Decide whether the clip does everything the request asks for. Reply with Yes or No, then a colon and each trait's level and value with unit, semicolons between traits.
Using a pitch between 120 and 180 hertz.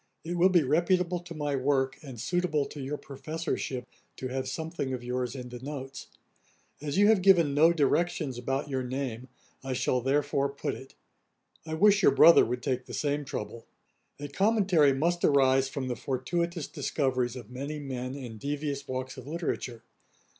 Yes: medium, 140 Hz